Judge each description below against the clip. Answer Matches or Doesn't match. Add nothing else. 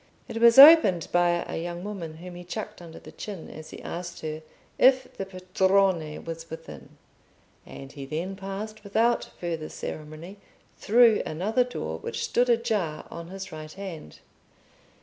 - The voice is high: Doesn't match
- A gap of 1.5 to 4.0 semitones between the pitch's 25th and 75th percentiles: Doesn't match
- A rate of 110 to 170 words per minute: Matches